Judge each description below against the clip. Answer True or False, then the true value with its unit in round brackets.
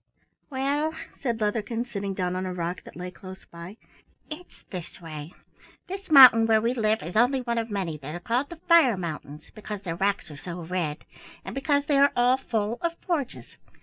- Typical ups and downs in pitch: False (6.6 semitones)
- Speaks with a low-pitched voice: False (215 Hz)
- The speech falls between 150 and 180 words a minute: False (195 wpm)